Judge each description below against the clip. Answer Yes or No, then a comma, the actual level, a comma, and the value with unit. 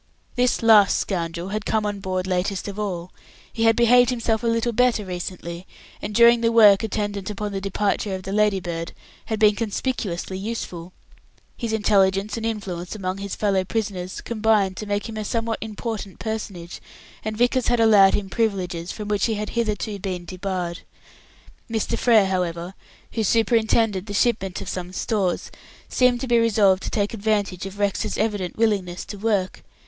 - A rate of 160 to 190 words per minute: Yes, average, 170 wpm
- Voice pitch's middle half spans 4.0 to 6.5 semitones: No, average, 3.0 semitones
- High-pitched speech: Yes, high, 205 Hz